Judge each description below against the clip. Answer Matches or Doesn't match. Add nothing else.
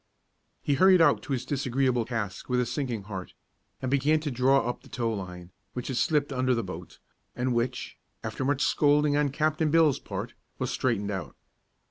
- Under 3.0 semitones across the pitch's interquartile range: Doesn't match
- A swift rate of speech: Doesn't match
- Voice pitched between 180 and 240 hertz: Doesn't match